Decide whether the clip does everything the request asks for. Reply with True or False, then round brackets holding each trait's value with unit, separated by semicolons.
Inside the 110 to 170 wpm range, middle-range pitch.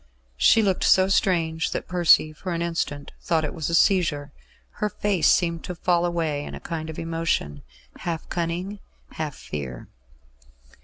True (160 wpm; 165 Hz)